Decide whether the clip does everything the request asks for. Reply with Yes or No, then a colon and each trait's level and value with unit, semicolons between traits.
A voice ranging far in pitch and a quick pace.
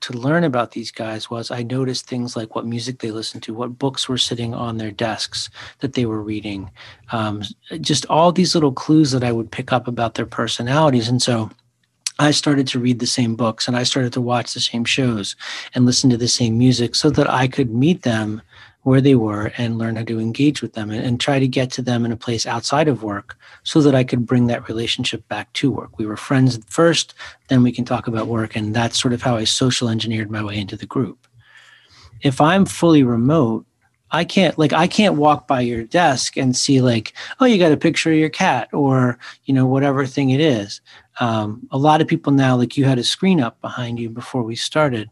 No: average, 3.4 semitones; fast, 230 wpm